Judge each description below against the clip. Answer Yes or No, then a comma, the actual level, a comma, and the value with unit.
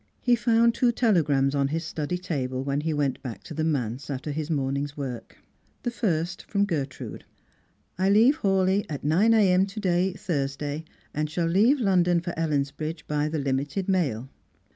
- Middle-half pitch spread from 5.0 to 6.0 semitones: Yes, average, 5.3 semitones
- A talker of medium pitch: Yes, medium, 160 Hz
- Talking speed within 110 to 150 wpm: No, average, 175 wpm